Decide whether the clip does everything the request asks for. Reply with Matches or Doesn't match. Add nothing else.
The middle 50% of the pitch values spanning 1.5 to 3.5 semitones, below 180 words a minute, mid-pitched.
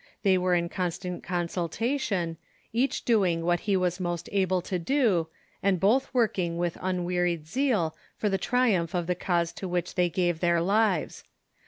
Matches